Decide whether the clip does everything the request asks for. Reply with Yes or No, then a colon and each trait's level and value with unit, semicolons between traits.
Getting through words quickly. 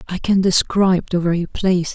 No: average, 185 wpm